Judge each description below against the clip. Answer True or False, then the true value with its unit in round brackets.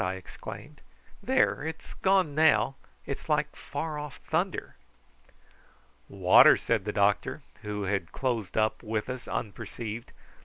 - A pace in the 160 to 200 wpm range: False (140 wpm)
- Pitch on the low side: True (115 Hz)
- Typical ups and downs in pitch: False (6.3 semitones)